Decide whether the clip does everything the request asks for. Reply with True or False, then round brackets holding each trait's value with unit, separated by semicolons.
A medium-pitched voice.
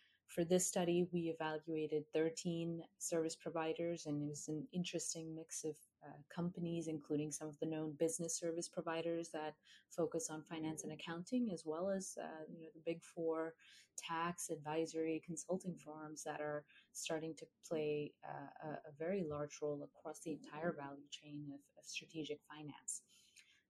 True (160 Hz)